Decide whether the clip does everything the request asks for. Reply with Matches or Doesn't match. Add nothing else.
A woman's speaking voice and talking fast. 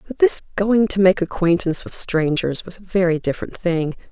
Doesn't match